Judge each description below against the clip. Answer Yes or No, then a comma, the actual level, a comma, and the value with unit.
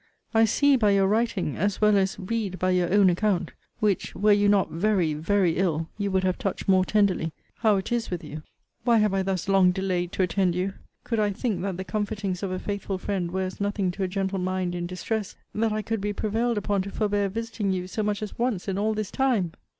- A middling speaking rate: No, fast, 235 wpm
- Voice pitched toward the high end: Yes, high, 195 Hz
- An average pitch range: No, narrow, 2.3 semitones